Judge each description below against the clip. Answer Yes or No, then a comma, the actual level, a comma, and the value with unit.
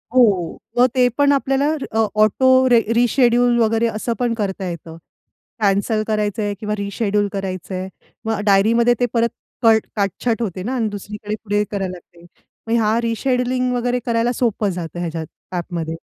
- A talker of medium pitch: No, high, 220 Hz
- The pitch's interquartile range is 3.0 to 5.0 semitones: Yes, average, 3.5 semitones